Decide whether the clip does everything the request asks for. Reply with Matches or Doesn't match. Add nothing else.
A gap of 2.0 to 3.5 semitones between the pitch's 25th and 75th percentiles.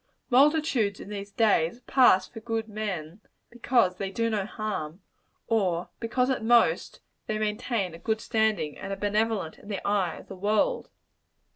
Matches